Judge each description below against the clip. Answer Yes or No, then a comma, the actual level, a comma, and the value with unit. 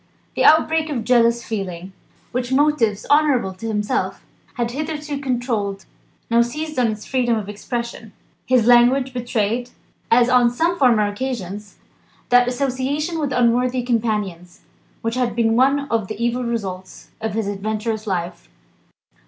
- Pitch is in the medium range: No, high, 235 Hz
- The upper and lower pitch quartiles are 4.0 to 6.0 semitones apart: No, average, 3.3 semitones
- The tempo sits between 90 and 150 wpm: Yes, average, 140 wpm